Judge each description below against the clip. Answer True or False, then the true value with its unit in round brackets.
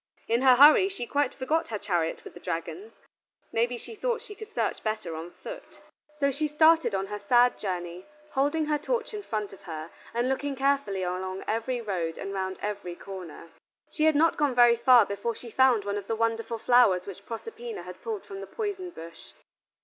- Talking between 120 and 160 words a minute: False (205 wpm)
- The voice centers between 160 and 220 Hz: False (235 Hz)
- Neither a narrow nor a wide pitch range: False (7.6 semitones)